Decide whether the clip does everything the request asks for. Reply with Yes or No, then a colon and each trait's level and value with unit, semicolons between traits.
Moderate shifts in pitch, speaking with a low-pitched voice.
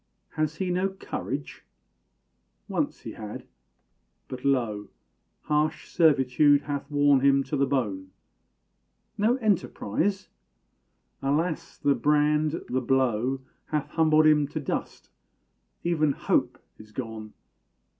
No: average, 3.1 semitones; medium, 145 Hz